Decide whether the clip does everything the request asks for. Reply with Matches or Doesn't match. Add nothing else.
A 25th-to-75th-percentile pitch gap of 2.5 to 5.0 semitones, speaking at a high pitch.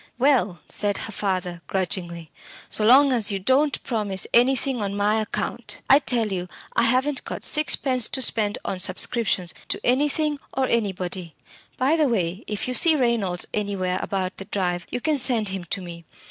Doesn't match